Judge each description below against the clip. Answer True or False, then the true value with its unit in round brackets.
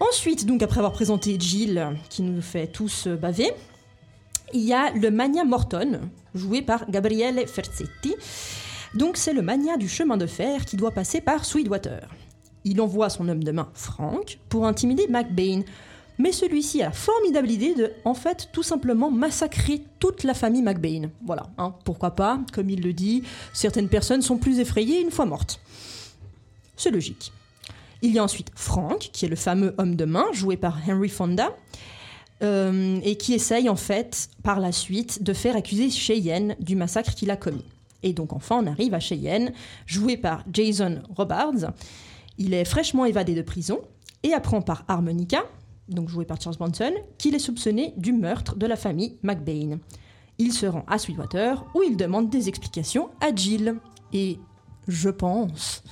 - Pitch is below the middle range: False (200 Hz)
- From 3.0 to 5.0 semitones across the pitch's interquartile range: False (5.6 semitones)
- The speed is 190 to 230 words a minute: False (175 wpm)